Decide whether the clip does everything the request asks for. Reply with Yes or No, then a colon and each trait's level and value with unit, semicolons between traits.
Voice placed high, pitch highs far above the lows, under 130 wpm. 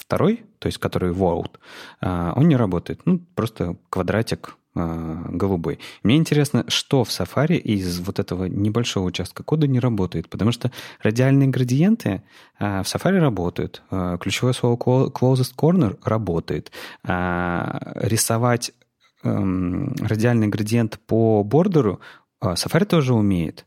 No: low, 115 Hz; wide, 6.4 semitones; average, 115 wpm